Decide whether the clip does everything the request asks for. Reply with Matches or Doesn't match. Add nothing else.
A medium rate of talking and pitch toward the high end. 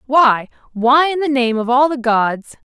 Matches